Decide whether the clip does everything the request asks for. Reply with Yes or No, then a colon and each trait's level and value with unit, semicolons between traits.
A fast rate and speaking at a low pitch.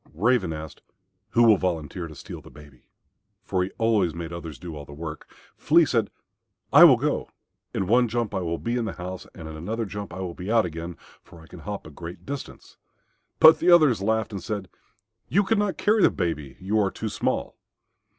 Yes: fast, 215 wpm; very low, 95 Hz